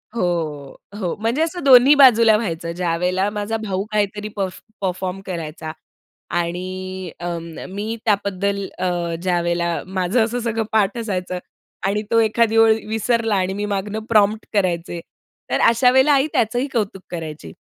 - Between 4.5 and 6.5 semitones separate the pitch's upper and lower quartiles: No, average, 3.8 semitones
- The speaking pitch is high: Yes, high, 200 Hz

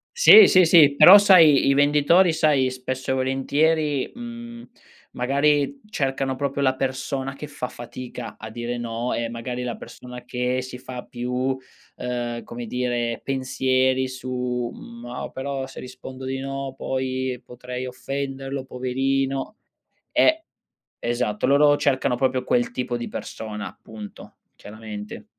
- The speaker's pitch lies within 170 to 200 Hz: No, low, 130 Hz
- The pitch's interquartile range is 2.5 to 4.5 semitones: No, narrow, 2.0 semitones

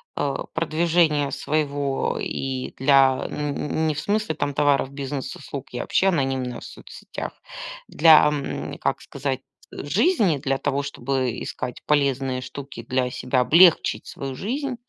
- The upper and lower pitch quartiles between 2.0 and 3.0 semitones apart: Yes, narrow, 2.6 semitones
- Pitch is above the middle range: No, medium, 140 Hz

